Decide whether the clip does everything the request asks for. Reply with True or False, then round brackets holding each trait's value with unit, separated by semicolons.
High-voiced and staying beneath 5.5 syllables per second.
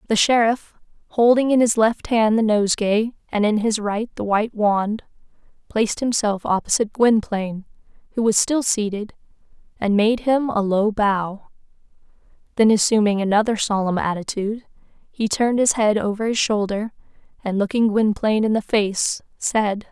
True (215 Hz; 5.0 syllables/s)